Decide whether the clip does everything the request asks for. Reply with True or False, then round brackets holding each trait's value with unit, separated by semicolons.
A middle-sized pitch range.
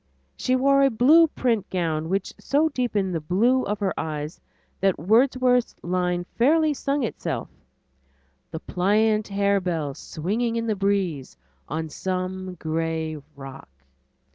False (6.7 semitones)